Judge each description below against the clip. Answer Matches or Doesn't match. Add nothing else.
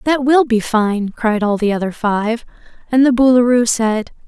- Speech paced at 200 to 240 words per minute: Doesn't match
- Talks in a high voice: Matches